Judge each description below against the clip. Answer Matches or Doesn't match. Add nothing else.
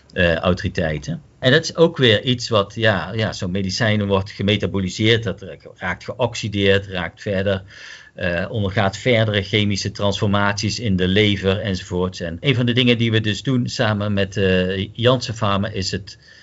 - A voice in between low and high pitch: Doesn't match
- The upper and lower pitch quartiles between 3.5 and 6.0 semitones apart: Doesn't match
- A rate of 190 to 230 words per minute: Doesn't match